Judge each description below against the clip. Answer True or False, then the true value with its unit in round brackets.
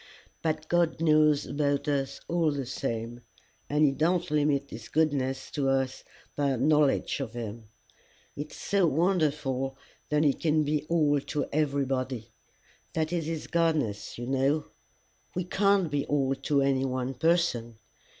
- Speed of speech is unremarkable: True (150 wpm)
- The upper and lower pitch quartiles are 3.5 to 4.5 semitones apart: False (2.9 semitones)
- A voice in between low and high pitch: True (145 Hz)